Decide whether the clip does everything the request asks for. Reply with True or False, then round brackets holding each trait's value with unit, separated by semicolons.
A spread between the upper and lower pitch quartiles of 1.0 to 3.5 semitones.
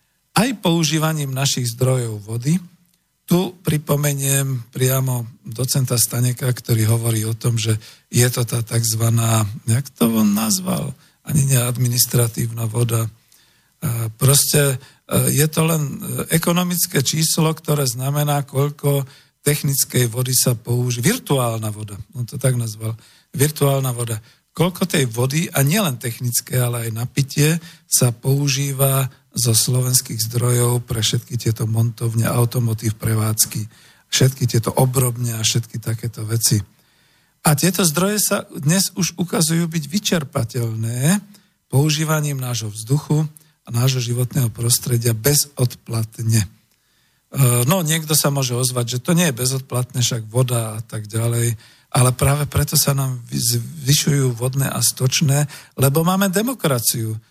False (4.3 semitones)